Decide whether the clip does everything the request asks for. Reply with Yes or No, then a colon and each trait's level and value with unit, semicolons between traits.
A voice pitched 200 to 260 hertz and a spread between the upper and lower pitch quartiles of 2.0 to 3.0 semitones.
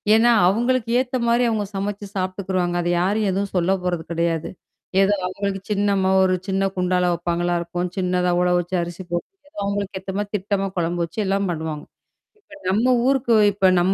No: high, 190 Hz; average, 2.7 semitones